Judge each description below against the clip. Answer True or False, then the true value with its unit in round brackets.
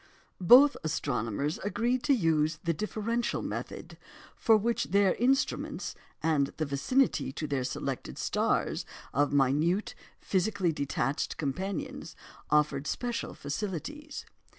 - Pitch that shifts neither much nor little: False (7.5 semitones)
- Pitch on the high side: False (170 Hz)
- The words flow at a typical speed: False (110 wpm)